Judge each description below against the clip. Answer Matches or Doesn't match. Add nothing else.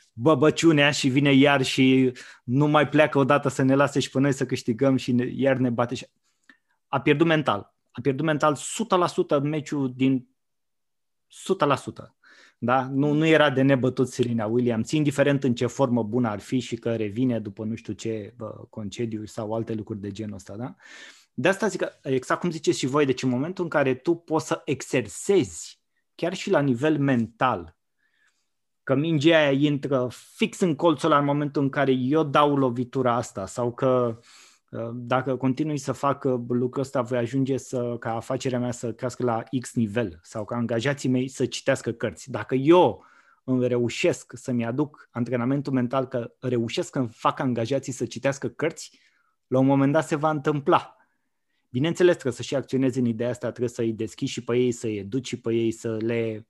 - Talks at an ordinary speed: Doesn't match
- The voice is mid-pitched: Doesn't match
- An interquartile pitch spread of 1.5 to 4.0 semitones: Matches